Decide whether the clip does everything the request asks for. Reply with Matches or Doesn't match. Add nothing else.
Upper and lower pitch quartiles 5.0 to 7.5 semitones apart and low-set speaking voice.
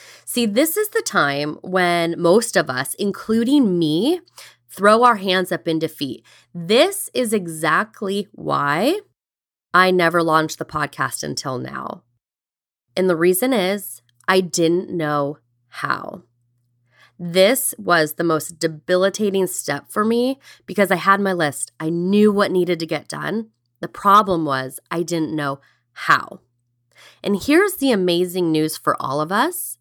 Doesn't match